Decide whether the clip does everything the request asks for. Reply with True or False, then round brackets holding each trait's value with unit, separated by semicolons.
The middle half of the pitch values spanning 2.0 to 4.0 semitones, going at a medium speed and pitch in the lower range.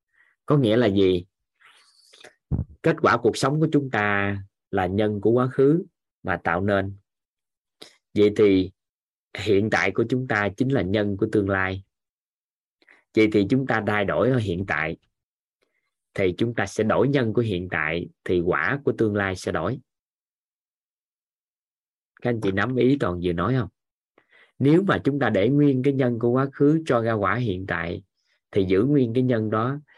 False (5.1 semitones; 175 wpm; 110 Hz)